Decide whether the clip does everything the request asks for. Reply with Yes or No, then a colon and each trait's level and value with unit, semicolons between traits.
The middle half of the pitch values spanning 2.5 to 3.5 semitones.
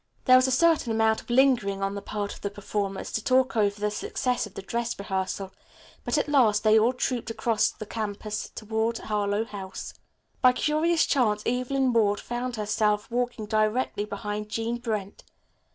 Yes: average, 3.2 semitones